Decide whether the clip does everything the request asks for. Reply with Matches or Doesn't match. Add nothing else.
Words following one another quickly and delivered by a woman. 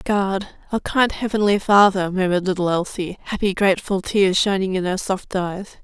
Doesn't match